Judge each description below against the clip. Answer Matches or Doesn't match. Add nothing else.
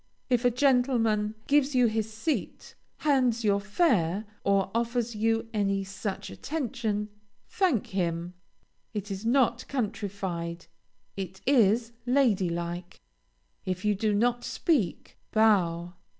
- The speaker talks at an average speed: Doesn't match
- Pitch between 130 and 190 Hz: Doesn't match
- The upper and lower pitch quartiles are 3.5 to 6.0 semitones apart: Matches